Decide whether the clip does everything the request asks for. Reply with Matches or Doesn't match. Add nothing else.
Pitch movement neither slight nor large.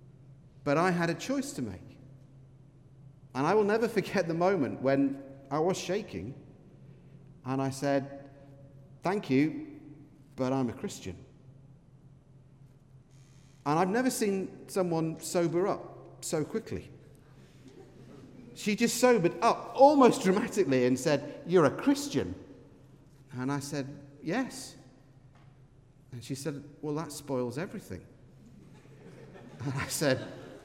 Matches